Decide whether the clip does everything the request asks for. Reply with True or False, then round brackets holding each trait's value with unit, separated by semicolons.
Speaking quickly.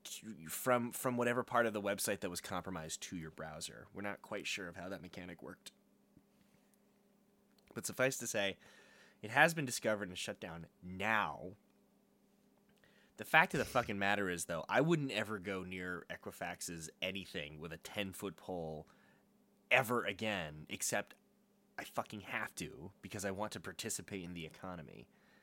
False (165 wpm)